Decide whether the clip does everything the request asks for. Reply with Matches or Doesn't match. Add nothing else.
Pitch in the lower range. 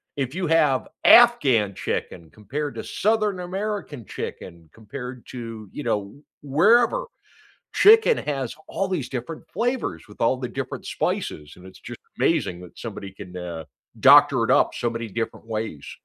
Matches